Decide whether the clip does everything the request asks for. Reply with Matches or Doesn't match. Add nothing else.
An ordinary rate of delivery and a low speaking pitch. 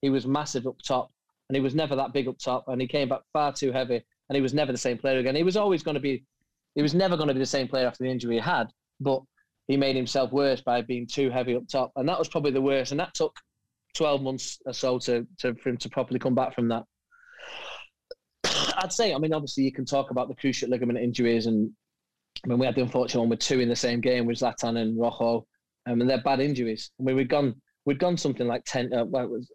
Doesn't match